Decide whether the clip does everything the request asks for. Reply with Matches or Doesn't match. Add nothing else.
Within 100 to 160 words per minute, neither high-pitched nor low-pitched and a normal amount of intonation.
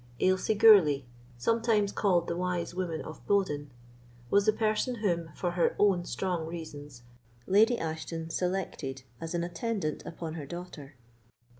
Matches